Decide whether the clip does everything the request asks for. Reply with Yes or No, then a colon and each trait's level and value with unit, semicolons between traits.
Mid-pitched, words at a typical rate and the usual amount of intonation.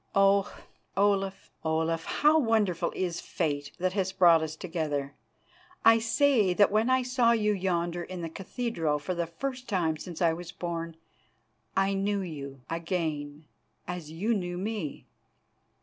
Yes: medium, 180 Hz; average, 150 wpm; average, 4.0 semitones